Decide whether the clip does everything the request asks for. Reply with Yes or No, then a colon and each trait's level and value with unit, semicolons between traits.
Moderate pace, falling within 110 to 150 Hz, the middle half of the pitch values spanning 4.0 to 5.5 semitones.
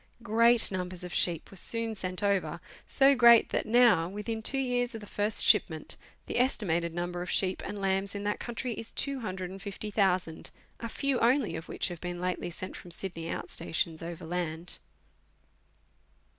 No: average, 165 wpm; high, 195 Hz; average, 4.5 semitones